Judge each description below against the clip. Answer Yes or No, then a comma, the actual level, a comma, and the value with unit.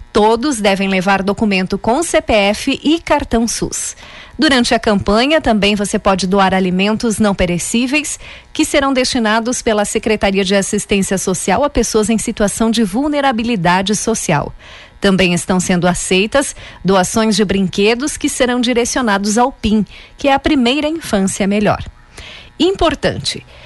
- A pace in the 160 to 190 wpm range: No, average, 135 wpm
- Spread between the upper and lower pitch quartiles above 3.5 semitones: Yes, average, 4.1 semitones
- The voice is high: Yes, high, 220 Hz